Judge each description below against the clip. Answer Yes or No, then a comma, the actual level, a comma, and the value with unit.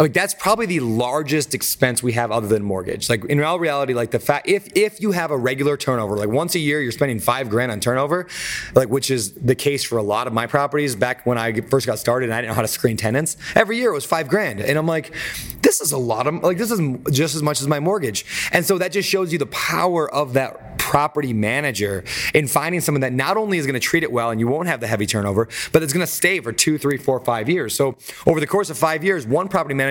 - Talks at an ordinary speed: No, fast, 270 wpm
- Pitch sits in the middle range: Yes, medium, 145 Hz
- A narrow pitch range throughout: No, average, 5.3 semitones